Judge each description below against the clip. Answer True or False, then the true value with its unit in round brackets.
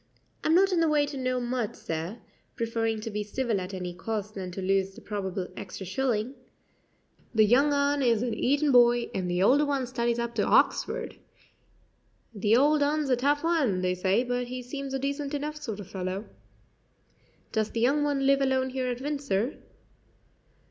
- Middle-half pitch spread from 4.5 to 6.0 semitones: True (5.1 semitones)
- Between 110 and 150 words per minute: False (185 wpm)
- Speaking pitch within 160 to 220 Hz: False (245 Hz)